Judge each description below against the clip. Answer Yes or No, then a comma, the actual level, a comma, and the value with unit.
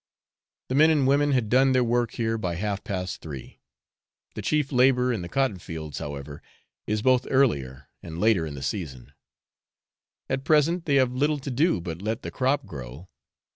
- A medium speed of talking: Yes, average, 180 wpm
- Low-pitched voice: Yes, low, 115 Hz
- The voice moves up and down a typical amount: No, wide, 8.0 semitones